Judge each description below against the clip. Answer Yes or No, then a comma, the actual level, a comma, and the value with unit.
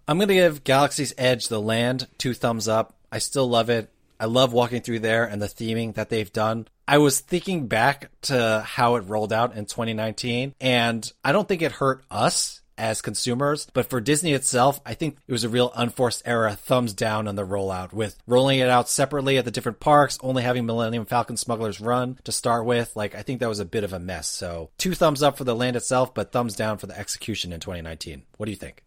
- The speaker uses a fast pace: Yes, fast, 230 wpm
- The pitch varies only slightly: No, average, 3.1 semitones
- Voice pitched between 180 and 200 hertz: No, low, 120 Hz